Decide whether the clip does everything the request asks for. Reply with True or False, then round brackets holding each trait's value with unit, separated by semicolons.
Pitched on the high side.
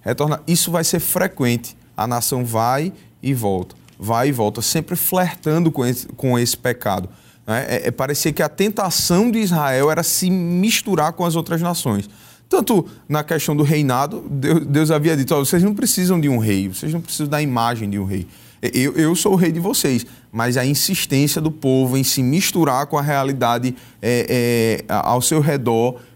False (145 Hz)